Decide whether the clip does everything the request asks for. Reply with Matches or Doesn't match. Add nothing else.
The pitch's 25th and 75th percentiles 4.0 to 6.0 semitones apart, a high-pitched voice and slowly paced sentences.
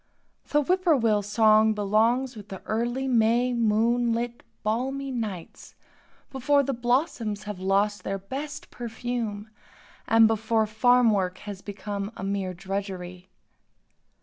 Doesn't match